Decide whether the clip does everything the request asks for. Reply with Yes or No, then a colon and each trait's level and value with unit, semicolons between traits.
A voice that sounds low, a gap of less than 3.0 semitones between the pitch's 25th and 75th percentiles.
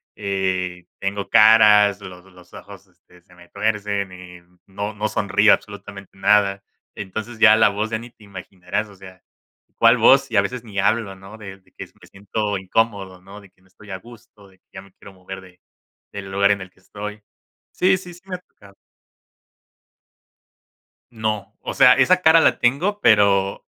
Yes: low, 100 Hz; narrow, 2.4 semitones